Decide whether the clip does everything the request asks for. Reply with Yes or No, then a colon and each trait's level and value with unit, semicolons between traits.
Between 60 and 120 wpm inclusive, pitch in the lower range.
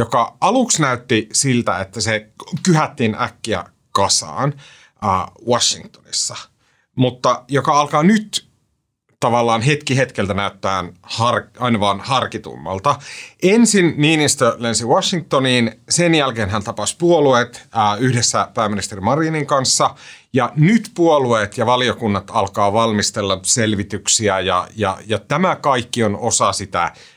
Yes: average, 110 wpm; low, 120 Hz